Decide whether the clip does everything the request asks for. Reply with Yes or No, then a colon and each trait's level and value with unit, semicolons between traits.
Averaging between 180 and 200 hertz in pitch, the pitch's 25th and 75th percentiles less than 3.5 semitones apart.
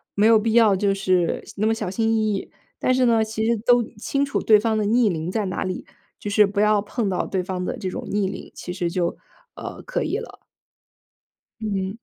No: high, 210 Hz; average, 2.8 semitones